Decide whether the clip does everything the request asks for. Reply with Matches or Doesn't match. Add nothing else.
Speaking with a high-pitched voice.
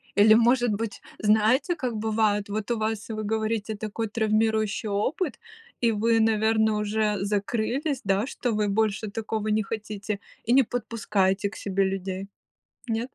Matches